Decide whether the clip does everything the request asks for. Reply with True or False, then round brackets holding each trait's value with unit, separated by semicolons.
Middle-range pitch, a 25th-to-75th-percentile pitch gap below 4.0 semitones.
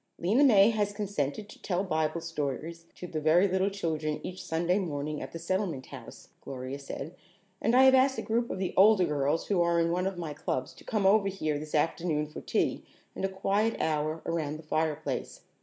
False (170 Hz; 4.3 semitones)